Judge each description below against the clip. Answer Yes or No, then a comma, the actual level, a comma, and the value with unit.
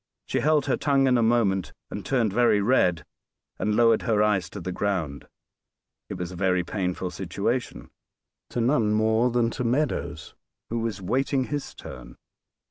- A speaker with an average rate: Yes, average, 165 wpm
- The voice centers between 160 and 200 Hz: No, low, 110 Hz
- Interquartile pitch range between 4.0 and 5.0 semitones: Yes, average, 4.7 semitones